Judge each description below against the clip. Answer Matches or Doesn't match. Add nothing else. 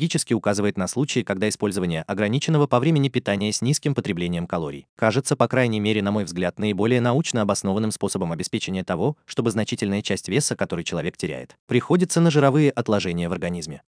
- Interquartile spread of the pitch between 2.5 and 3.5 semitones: Doesn't match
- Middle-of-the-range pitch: Doesn't match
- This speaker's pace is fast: Matches